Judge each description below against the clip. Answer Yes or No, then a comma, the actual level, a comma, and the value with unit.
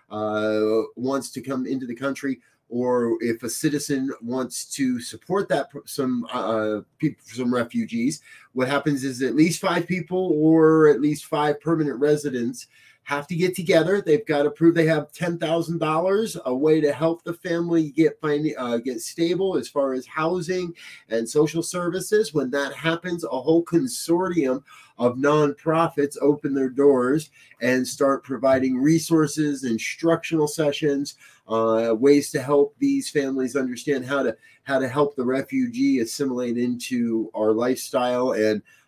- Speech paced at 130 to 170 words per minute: Yes, average, 155 wpm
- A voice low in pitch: No, medium, 145 Hz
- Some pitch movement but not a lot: Yes, average, 4.2 semitones